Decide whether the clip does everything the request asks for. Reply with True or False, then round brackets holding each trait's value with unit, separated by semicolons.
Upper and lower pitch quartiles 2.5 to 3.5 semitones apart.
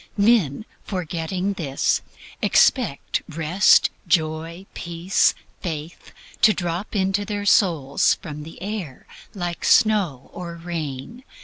False (3.9 semitones)